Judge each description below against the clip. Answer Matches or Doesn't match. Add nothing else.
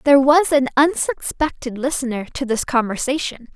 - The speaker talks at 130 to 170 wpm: Matches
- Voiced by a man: Doesn't match